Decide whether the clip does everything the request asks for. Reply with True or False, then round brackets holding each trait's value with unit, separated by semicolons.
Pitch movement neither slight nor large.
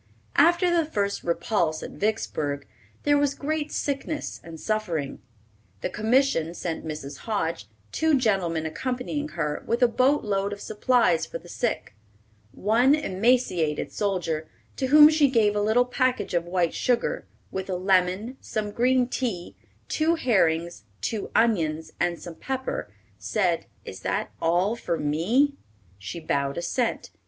False (7.3 semitones)